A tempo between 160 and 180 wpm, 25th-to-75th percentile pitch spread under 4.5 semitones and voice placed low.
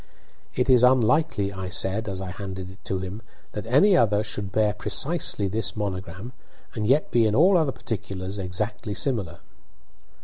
Yes: average, 165 wpm; average, 4.0 semitones; low, 105 Hz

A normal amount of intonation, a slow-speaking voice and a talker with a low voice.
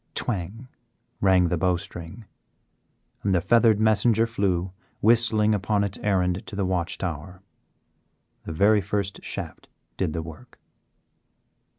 Yes: average, 3.2 semitones; slow, 120 wpm; low, 100 Hz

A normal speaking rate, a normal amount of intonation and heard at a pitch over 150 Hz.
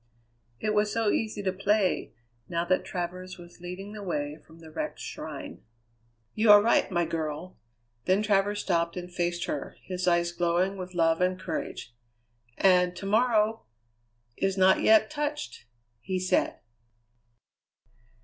Yes: average, 145 wpm; average, 3.1 semitones; medium, 185 Hz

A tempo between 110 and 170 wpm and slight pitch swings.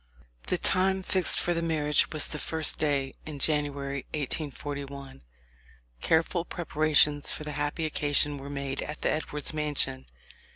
Yes: average, 140 wpm; narrow, 1.8 semitones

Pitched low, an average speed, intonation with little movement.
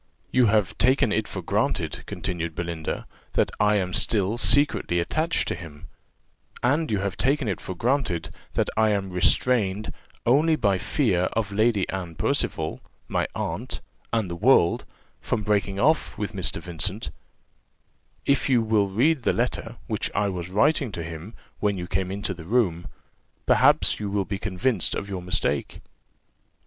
No: low, 100 Hz; average, 155 wpm; average, 4.6 semitones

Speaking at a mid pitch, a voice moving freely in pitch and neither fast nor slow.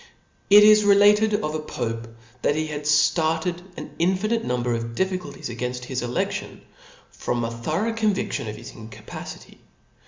Yes: medium, 155 Hz; wide, 8.8 semitones; average, 155 wpm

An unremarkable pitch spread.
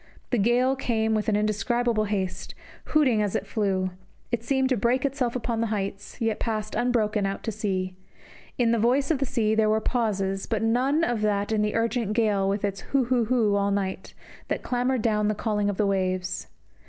Yes: average, 3.0 semitones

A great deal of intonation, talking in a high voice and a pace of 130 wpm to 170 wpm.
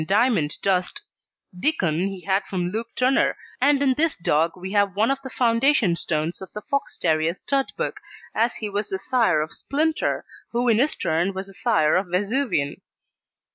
No: wide, 6.1 semitones; high, 200 Hz; average, 180 wpm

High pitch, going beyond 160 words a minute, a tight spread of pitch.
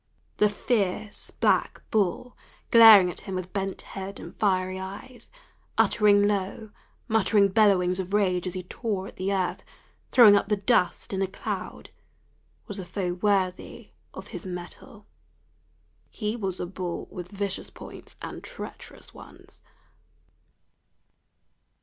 No: high, 195 Hz; slow, 135 wpm; narrow, 2.1 semitones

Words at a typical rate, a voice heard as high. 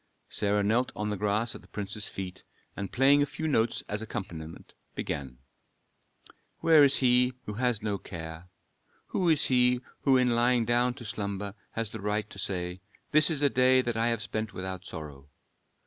No: average, 180 wpm; low, 110 Hz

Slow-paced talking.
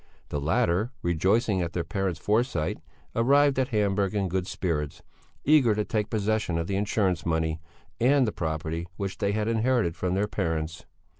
No: average, 165 wpm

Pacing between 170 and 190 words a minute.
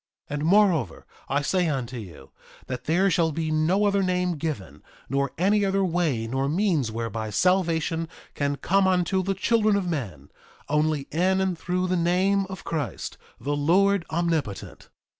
No: average, 160 wpm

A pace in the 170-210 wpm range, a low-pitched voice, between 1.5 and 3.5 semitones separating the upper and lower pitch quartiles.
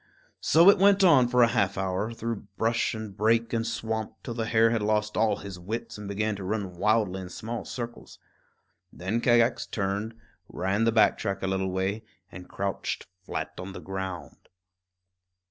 Yes: average, 180 wpm; low, 110 Hz; average, 3.1 semitones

